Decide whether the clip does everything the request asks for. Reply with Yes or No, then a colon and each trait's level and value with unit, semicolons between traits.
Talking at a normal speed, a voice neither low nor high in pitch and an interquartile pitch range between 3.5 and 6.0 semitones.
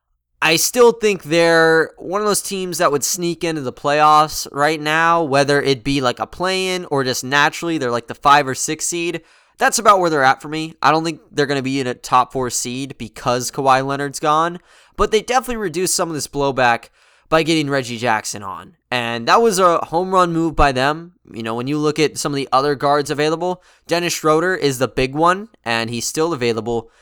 No: fast, 220 wpm; medium, 150 Hz; average, 4.3 semitones